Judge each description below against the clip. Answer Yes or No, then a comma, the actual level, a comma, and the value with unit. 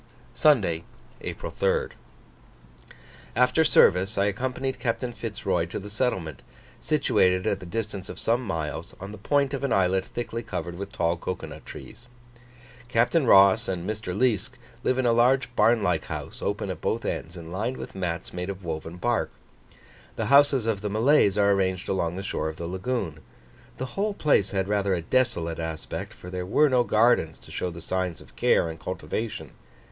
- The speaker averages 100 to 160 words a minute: No, average, 185 wpm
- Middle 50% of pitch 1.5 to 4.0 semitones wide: No, average, 5.1 semitones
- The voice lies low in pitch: Yes, low, 100 Hz